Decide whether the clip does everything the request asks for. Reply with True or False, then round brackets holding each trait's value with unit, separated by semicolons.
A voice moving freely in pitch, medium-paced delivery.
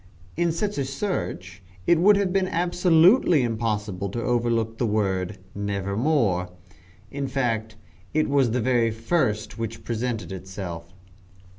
False (7.3 semitones; 130 wpm)